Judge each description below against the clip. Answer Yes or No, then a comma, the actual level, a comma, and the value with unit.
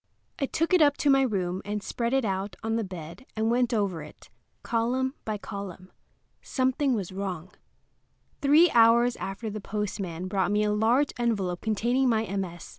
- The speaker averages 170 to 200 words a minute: Yes, average, 175 wpm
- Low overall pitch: No, high, 215 Hz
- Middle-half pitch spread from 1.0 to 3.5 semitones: No, average, 4.2 semitones